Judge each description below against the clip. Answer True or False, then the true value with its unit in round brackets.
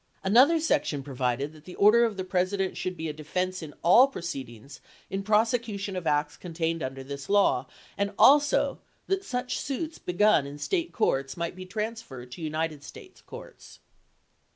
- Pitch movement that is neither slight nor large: False (6.8 semitones)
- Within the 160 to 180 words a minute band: True (165 wpm)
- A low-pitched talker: False (185 Hz)